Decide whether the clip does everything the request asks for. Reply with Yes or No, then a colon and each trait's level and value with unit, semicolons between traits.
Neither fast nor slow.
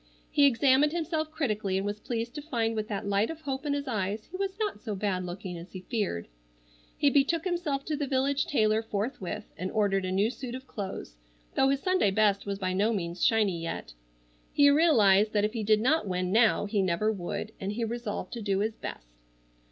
No: fast, 215 wpm